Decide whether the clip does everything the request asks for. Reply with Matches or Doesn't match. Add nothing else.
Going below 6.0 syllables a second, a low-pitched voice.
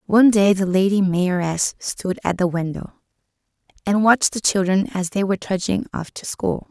Doesn't match